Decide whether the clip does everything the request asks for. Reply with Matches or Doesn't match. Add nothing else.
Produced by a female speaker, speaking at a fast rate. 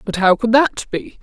Matches